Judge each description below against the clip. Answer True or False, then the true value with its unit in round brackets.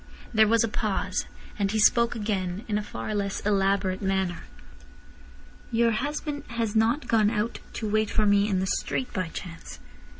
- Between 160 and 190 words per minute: True (170 wpm)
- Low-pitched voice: False (210 Hz)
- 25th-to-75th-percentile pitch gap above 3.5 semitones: False (2.7 semitones)